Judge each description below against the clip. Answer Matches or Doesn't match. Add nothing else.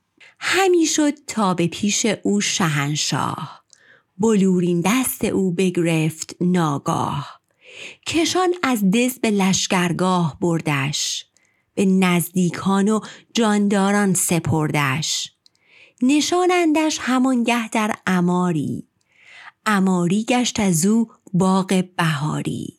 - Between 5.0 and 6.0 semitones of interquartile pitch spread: Matches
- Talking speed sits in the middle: Doesn't match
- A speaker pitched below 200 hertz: Matches